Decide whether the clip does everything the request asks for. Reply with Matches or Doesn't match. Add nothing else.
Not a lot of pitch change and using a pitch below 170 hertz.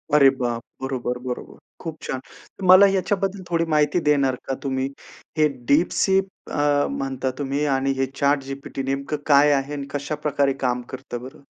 Matches